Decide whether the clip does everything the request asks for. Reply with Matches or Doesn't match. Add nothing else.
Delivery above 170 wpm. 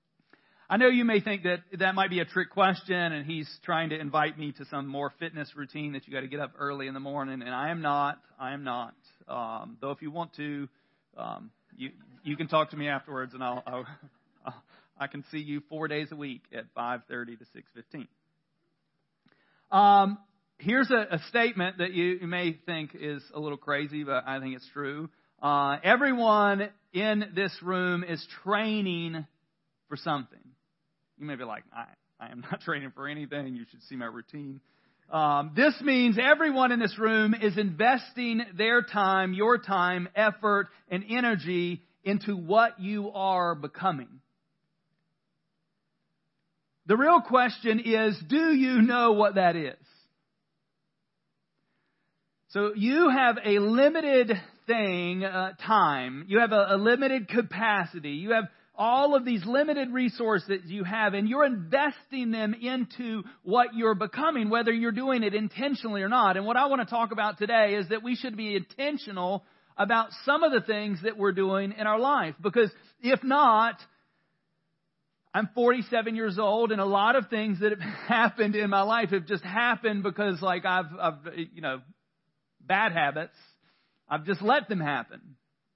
Doesn't match